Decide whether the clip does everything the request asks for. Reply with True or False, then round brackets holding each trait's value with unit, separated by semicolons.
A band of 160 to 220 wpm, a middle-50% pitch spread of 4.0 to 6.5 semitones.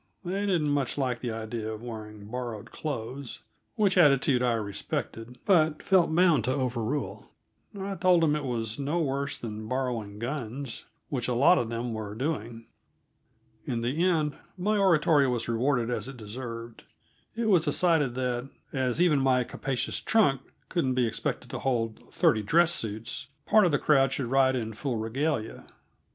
True (165 wpm; 4.7 semitones)